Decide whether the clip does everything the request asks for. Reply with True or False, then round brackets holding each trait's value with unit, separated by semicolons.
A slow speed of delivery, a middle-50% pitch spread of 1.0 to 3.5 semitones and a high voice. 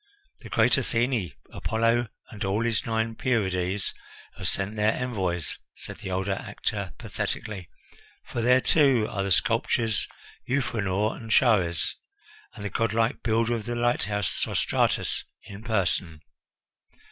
False (130 wpm; 3.2 semitones; 110 Hz)